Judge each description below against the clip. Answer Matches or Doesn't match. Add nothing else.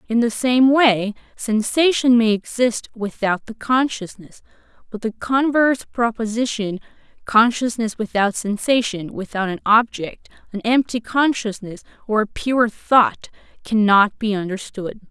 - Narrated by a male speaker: Doesn't match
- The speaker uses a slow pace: Matches